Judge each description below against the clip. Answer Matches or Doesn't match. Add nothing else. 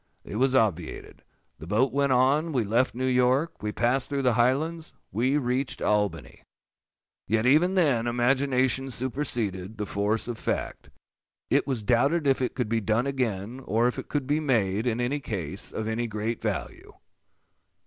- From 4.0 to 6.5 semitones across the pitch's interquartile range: Doesn't match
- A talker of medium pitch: Doesn't match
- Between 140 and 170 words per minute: Matches